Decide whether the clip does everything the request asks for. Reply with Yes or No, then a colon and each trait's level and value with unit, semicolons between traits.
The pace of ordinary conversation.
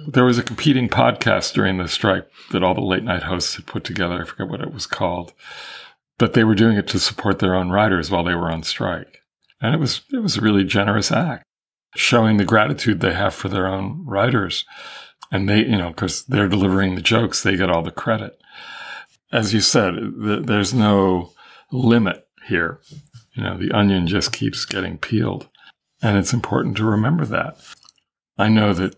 Yes: average, 195 wpm